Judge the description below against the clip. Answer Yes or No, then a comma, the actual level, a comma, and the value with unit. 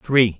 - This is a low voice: Yes, low, 110 Hz